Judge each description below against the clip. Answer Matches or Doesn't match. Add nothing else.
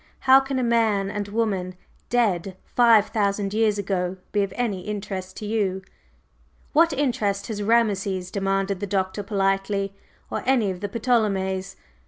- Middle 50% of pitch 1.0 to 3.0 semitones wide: Matches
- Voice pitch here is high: Matches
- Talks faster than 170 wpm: Doesn't match